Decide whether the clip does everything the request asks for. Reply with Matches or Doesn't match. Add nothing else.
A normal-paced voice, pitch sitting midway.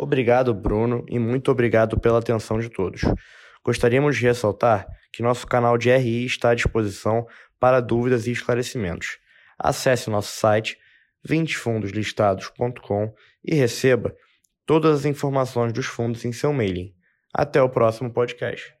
Doesn't match